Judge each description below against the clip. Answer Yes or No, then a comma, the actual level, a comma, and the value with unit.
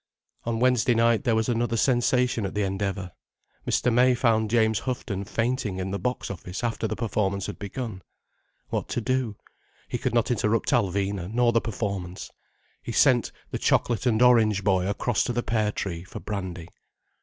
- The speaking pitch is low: Yes, low, 110 Hz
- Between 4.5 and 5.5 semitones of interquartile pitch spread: No, average, 3.5 semitones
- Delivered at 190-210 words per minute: No, average, 175 wpm